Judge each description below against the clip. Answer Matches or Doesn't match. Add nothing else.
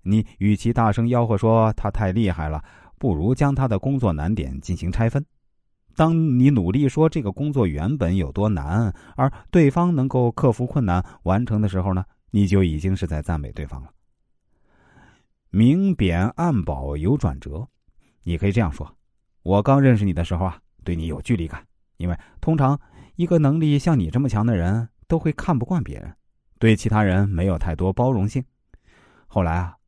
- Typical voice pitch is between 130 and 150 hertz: Doesn't match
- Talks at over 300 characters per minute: Doesn't match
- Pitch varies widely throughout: Matches